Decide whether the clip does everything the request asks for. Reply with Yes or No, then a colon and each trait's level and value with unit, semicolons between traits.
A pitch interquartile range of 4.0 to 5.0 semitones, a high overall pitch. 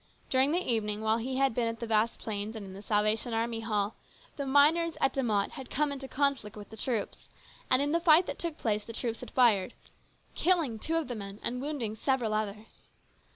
Yes: average, 4.4 semitones; high, 230 Hz